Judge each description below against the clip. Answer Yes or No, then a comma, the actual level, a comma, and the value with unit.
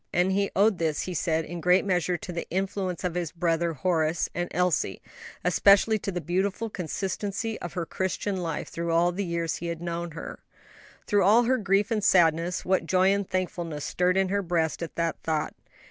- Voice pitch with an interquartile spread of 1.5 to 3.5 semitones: Yes, narrow, 2.5 semitones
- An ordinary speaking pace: Yes, average, 195 wpm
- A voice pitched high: No, medium, 180 Hz